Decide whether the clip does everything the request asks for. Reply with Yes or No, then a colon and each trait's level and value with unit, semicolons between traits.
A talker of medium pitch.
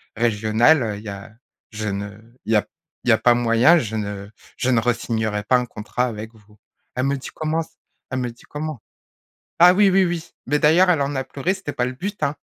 No: low, 125 Hz